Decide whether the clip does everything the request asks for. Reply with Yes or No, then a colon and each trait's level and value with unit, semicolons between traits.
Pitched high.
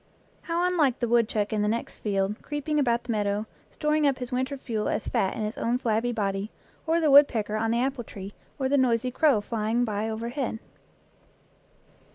Yes: high, 235 Hz